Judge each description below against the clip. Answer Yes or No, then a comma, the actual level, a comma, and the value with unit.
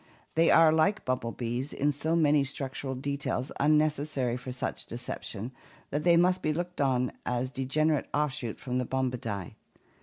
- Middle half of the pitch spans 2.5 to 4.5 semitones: Yes, average, 3.4 semitones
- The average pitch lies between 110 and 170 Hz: Yes, low, 135 Hz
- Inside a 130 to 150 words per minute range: No, average, 160 wpm